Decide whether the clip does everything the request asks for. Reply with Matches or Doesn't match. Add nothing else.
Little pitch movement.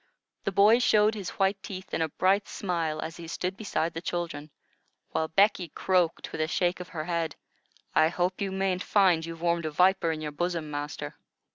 Doesn't match